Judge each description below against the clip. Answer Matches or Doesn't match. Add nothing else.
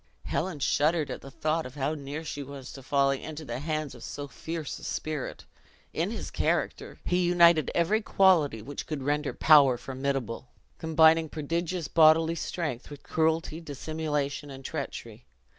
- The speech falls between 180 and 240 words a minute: Doesn't match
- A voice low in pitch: Doesn't match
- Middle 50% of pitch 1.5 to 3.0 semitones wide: Matches